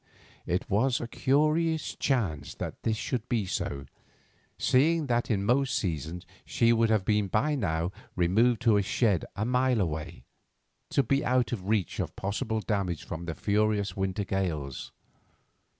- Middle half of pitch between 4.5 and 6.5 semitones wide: Yes, average, 5.2 semitones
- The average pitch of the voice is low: Yes, low, 105 Hz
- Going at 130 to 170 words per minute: Yes, average, 155 wpm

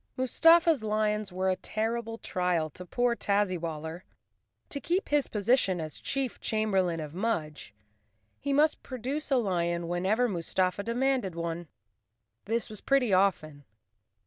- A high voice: Yes, high, 205 Hz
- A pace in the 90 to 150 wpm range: Yes, average, 140 wpm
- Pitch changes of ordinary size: No, wide, 6.0 semitones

